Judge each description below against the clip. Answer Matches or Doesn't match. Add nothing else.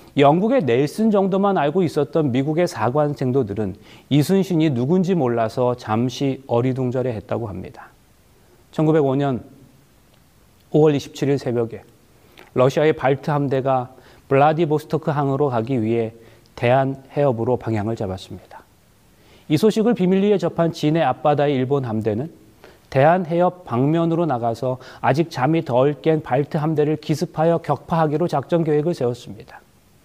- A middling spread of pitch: Matches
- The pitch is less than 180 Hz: Matches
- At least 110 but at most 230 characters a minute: Doesn't match